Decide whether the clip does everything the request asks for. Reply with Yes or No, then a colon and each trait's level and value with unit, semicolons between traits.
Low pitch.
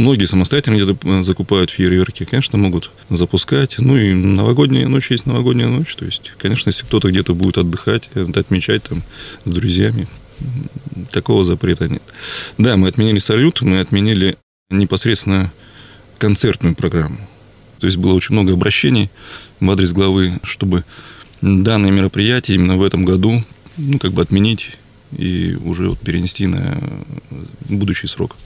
Yes: low, 100 Hz